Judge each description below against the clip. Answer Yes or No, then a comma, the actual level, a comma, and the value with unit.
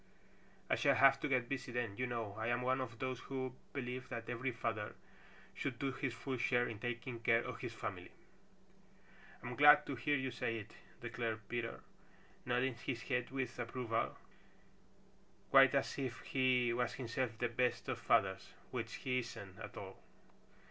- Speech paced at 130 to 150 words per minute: No, average, 170 wpm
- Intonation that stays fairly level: Yes, narrow, 2.1 semitones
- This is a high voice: No, low, 120 Hz